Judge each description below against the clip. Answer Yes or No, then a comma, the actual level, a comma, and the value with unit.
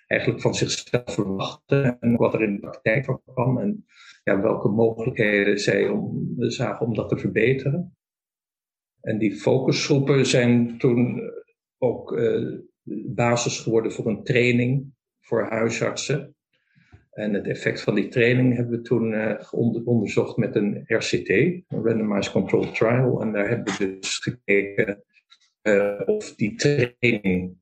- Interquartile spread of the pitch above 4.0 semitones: No, average, 3.5 semitones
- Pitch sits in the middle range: No, low, 120 Hz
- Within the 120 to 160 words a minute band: Yes, average, 140 wpm